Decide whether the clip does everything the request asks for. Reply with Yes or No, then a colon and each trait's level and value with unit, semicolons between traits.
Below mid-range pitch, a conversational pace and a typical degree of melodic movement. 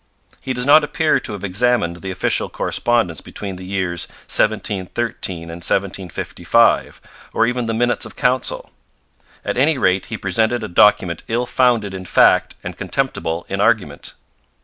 Yes: low, 105 Hz; average, 150 wpm; average, 4.8 semitones